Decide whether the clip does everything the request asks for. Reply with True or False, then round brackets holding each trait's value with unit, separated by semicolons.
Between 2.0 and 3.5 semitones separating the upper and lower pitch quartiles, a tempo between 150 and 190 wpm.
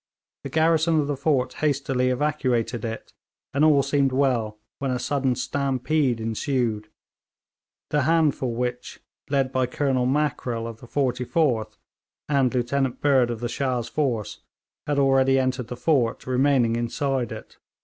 False (2.7 semitones; 140 wpm)